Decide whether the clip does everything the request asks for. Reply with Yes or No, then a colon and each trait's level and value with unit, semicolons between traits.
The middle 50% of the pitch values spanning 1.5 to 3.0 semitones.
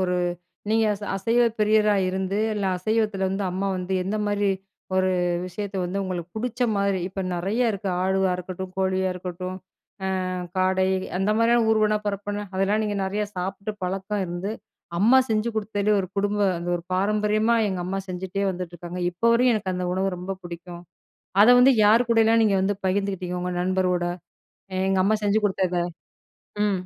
Yes: narrow, 2.4 semitones